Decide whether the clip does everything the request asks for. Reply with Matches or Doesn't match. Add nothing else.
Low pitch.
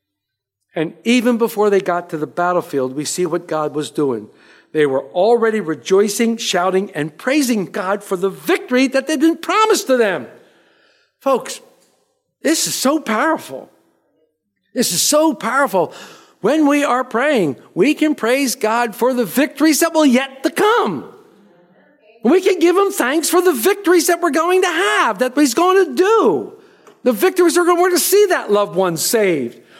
Doesn't match